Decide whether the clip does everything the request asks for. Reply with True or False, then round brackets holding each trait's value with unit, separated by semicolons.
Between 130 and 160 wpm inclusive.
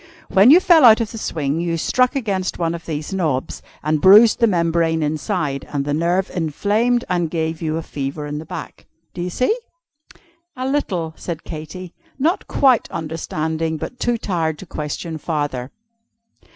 False (170 wpm)